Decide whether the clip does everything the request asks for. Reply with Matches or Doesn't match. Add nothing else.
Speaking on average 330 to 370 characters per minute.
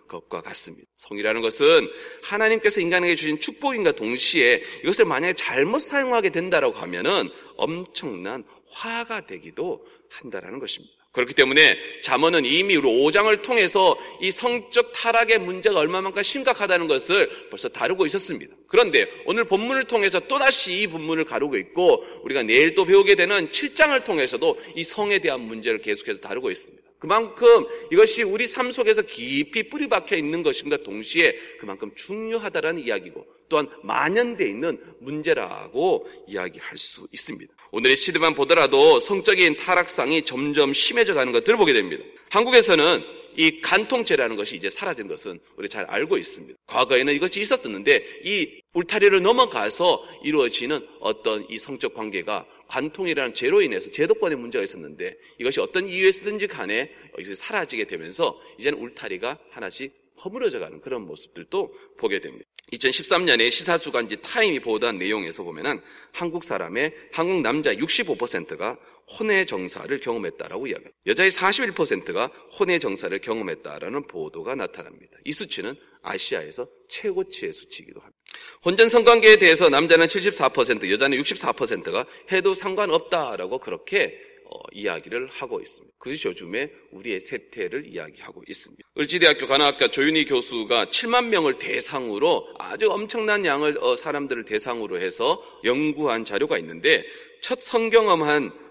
Matches